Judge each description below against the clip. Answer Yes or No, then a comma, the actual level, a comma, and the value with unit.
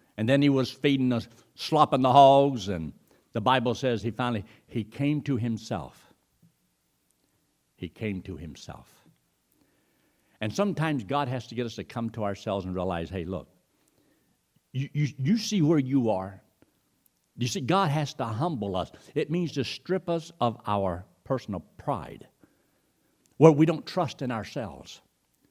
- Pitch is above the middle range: No, low, 125 Hz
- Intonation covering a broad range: Yes, wide, 6.0 semitones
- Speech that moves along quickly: No, average, 160 wpm